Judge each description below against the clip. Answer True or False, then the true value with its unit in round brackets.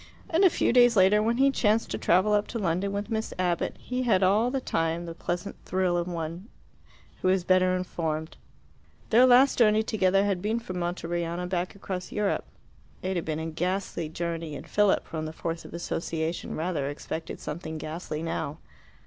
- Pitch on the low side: False (185 Hz)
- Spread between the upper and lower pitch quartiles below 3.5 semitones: False (3.9 semitones)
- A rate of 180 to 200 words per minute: True (185 wpm)